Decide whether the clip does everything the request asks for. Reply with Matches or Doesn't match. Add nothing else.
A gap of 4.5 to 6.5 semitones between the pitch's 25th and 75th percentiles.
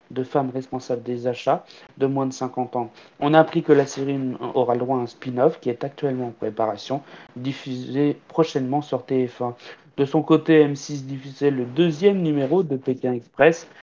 Doesn't match